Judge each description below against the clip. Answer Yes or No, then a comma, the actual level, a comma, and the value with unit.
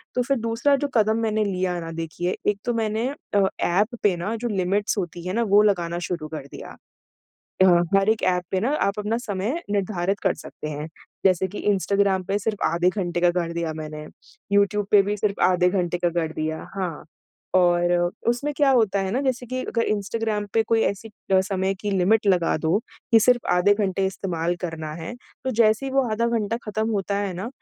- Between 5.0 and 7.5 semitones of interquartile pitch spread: No, average, 3.7 semitones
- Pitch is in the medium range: No, high, 200 Hz